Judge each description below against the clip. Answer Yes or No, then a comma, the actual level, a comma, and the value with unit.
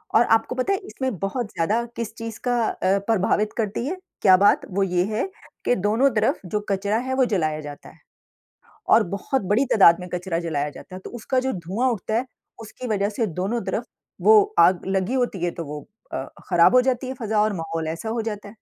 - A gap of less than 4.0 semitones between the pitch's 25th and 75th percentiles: No, average, 4.6 semitones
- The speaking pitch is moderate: No, high, 210 Hz